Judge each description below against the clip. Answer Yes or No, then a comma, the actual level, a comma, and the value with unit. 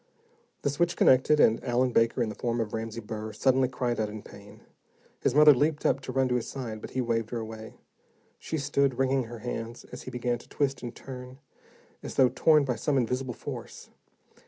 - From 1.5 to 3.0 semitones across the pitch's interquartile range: Yes, average, 2.7 semitones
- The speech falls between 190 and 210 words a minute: Yes, fast, 205 wpm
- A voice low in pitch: Yes, low, 125 Hz